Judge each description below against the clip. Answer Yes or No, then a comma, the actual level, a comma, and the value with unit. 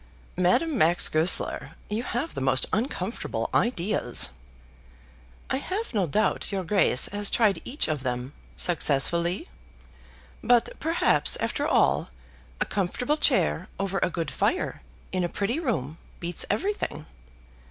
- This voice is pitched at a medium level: No, high, 195 Hz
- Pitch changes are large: Yes, wide, 6.5 semitones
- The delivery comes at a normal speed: No, slow, 130 wpm